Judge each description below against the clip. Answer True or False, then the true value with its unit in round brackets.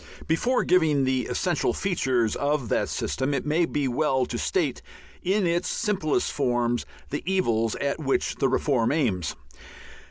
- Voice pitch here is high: False (140 Hz)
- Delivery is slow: False (150 wpm)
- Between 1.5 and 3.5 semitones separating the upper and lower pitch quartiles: False (4.6 semitones)